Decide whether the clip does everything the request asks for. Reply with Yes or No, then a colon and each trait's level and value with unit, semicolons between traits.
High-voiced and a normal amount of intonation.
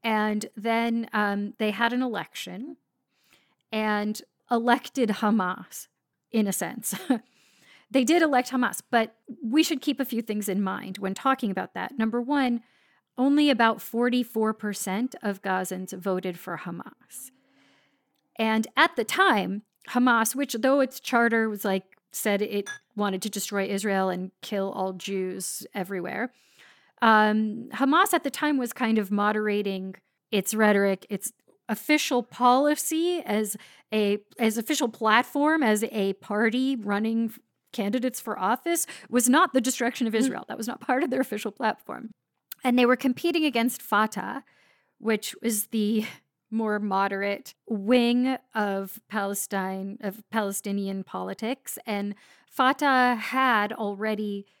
Yes: high, 225 Hz; average, 3.7 semitones